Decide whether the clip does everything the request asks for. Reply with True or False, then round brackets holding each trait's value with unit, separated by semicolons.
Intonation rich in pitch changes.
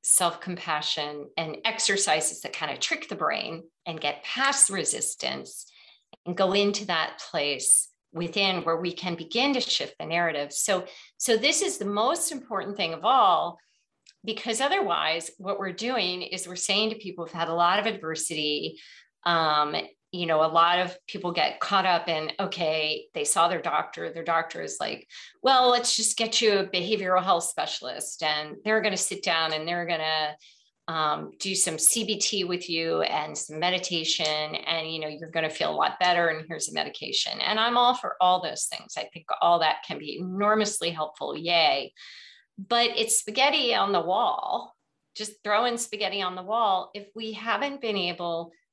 False (4.9 semitones)